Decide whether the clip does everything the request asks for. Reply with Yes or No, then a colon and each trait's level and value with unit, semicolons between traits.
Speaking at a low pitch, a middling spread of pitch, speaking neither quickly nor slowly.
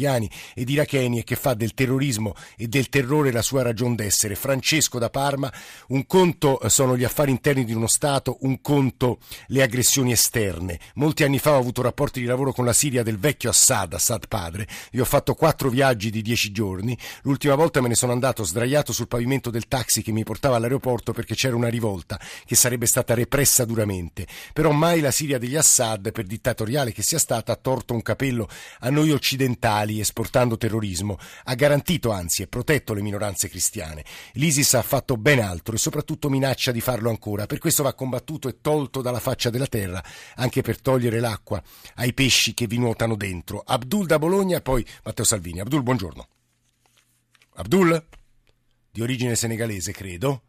No: low, 125 Hz; average, 3.4 semitones; fast, 180 wpm